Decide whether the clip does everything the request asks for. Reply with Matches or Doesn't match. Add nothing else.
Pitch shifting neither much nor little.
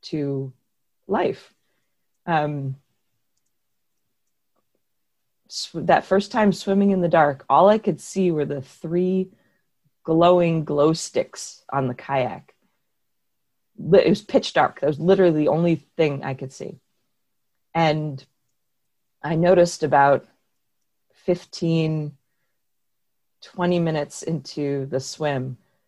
Matches